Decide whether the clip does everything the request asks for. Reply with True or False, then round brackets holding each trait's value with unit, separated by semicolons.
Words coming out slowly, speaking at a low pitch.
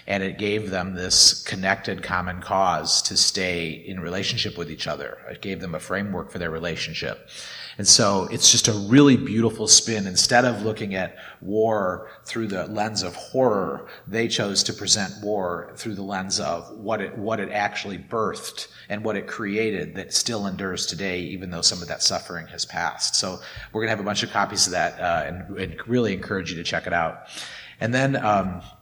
False (200 wpm; 100 Hz)